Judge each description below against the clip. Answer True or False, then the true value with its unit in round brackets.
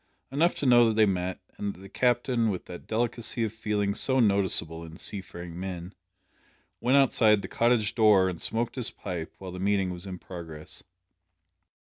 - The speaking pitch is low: True (100 Hz)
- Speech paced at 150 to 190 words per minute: True (180 wpm)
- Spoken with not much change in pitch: False (4.3 semitones)